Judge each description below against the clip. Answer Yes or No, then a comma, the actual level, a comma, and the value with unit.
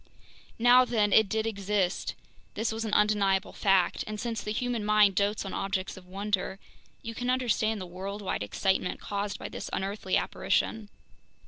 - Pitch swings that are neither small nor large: No, narrow, 2.2 semitones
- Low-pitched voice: No, high, 205 Hz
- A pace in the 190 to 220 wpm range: No, average, 160 wpm